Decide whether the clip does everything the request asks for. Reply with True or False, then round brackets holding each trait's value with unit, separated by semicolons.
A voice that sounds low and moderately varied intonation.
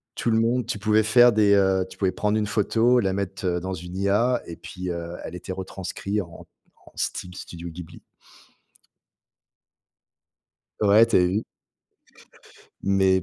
True (95 Hz; 3.0 semitones)